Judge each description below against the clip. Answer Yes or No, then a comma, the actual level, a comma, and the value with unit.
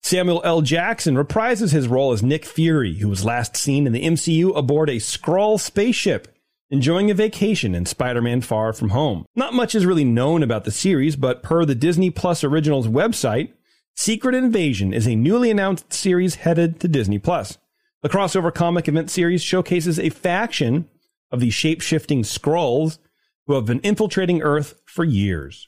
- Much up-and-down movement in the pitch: Yes, wide, 5.8 semitones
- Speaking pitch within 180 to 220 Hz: No, medium, 160 Hz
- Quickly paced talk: No, average, 170 wpm